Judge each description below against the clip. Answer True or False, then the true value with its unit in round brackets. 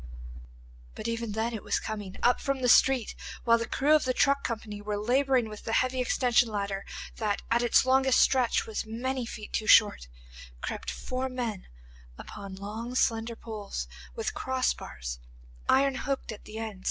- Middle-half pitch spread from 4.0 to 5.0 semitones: False (3.3 semitones)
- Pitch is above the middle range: True (230 Hz)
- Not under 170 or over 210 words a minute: True (175 wpm)